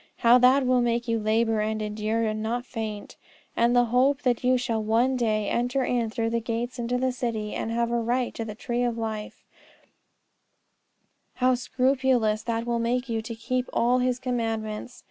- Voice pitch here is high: Yes, high, 235 Hz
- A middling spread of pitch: No, narrow, 2.0 semitones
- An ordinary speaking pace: Yes, average, 185 wpm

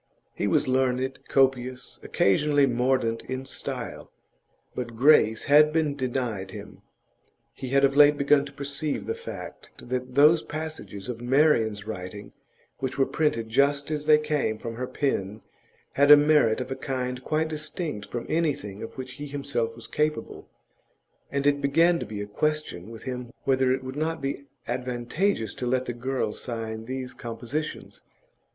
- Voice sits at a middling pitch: No, low, 130 Hz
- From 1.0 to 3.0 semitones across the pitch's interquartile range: No, average, 3.7 semitones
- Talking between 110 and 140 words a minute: No, average, 160 wpm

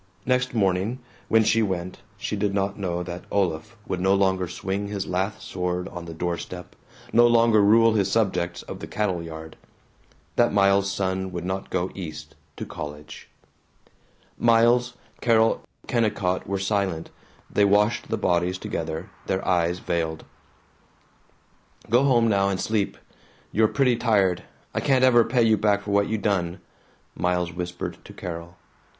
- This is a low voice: Yes, low, 100 Hz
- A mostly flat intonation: No, average, 3.7 semitones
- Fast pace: No, average, 155 wpm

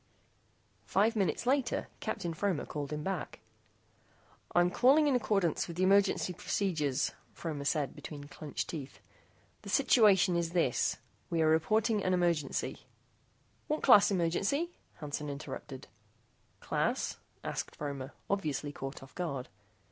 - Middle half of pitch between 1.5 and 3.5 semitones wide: No, average, 5.3 semitones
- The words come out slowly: Yes, slow, 130 wpm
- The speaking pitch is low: No, medium, 170 Hz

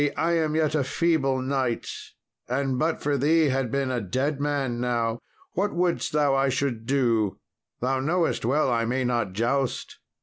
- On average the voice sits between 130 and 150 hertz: Yes, low, 135 Hz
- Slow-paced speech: No, average, 170 wpm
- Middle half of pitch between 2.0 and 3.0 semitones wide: No, average, 3.5 semitones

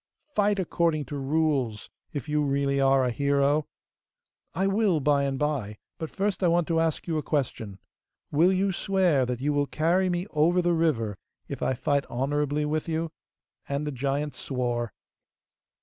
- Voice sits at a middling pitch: Yes, medium, 150 Hz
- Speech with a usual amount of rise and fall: Yes, average, 3.4 semitones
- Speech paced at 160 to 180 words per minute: Yes, average, 170 wpm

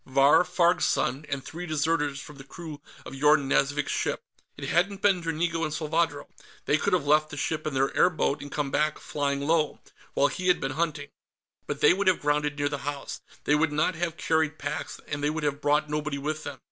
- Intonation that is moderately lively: No, narrow, 2.3 semitones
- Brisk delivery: Yes, fast, 215 wpm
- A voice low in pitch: No, medium, 150 Hz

